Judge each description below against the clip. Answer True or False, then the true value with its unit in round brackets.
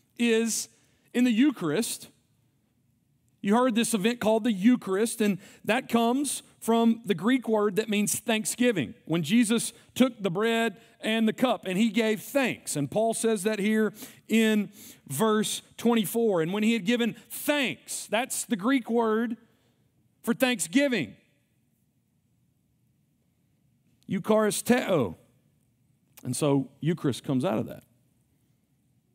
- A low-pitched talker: False (225 Hz)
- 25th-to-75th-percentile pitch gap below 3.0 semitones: True (2.4 semitones)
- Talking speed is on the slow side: True (130 wpm)